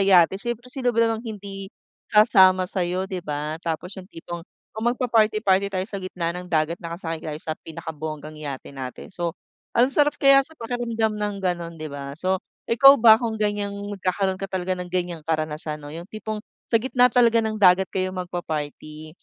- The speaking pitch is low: No, medium, 185 Hz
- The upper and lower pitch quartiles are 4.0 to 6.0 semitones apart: Yes, average, 4.8 semitones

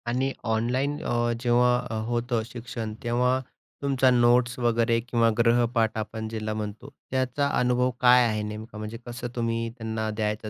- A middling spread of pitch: No, narrow, 1.8 semitones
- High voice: No, low, 120 Hz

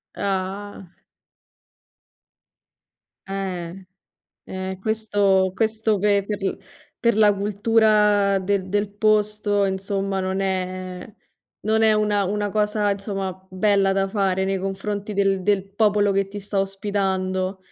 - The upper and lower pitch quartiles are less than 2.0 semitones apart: Yes, narrow, 1.5 semitones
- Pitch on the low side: No, high, 200 Hz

